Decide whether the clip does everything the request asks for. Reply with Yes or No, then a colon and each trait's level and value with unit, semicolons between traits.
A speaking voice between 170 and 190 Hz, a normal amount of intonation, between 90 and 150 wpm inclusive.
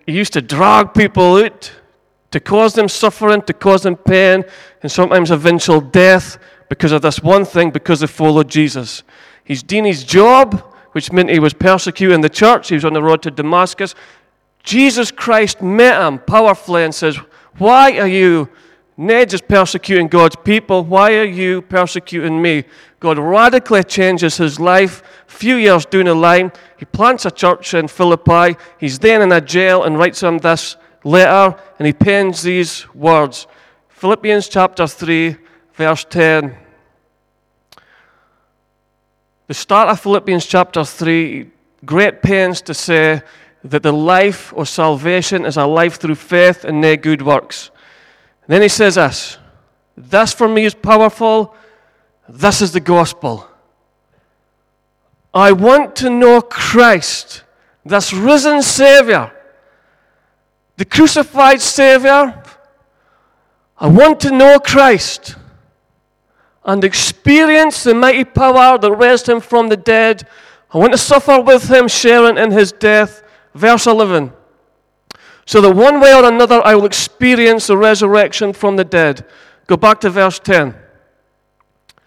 Yes: medium, 185 Hz; average, 4.8 semitones; average, 145 wpm